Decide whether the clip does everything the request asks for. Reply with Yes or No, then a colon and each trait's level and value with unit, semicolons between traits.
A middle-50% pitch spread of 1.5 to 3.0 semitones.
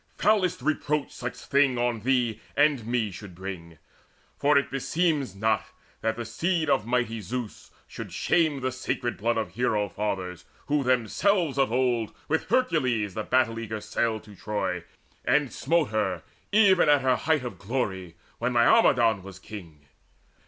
No: average, 4.9 semitones